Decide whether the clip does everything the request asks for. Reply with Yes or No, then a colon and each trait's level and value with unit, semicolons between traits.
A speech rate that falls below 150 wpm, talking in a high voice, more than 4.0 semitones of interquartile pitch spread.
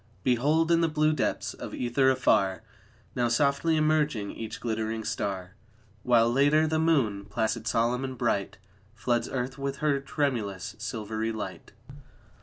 No: average, 140 wpm; low, 125 Hz; average, 4.7 semitones